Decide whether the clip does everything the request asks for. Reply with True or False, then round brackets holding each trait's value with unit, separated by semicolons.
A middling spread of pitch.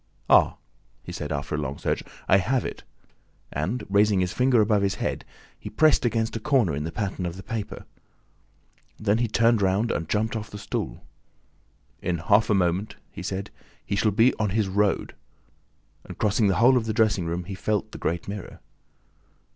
True (3.1 semitones)